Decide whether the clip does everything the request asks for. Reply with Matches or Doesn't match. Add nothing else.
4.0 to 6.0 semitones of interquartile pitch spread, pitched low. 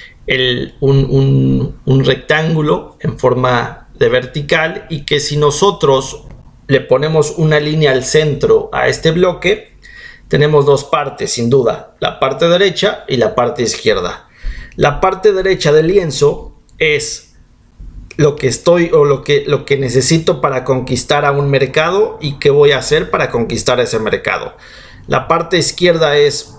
Doesn't match